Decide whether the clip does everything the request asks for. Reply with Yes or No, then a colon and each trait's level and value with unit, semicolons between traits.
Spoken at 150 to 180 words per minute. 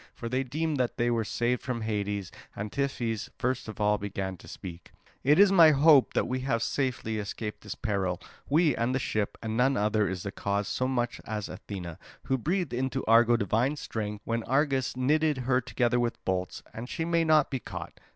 No: average, 200 wpm